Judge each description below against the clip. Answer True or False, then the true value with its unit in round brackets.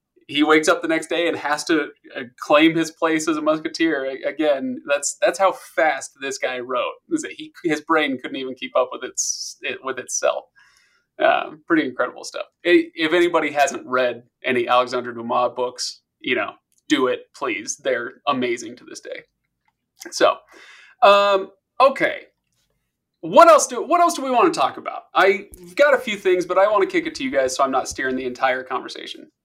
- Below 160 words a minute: False (185 wpm)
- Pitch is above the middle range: True (195 Hz)